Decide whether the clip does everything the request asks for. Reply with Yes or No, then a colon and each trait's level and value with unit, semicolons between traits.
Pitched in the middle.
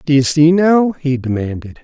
Yes: medium, 145 Hz